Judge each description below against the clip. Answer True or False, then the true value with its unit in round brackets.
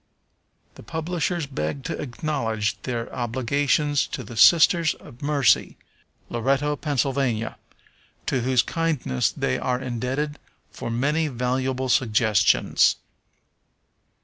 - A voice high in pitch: False (130 Hz)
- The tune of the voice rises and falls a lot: False (3.8 semitones)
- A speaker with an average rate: False (100 wpm)